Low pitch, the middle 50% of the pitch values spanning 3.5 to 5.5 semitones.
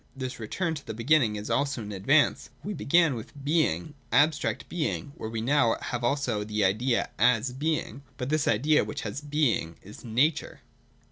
Yes: low, 130 Hz; average, 5.1 semitones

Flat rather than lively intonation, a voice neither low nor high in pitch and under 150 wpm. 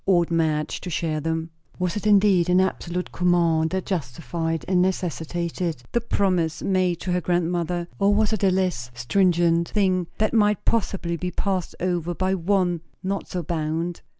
No: narrow, 2.2 semitones; medium, 175 Hz; average, 165 wpm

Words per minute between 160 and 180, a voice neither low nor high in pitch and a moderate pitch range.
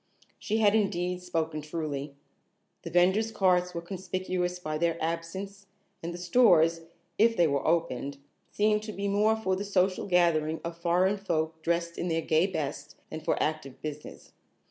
Yes: average, 165 wpm; medium, 175 Hz; average, 3.2 semitones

